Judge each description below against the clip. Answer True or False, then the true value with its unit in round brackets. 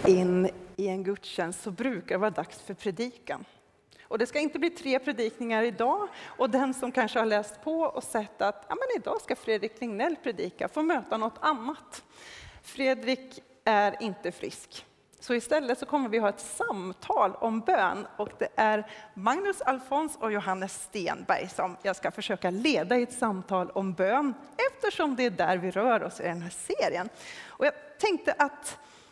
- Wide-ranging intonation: True (6.0 semitones)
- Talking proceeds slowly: False (180 wpm)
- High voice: True (230 Hz)